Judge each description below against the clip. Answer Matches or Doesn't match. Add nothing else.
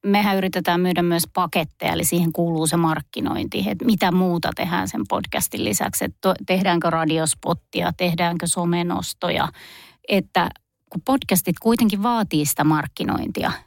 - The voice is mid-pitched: Matches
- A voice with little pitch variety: Matches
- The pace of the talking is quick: Doesn't match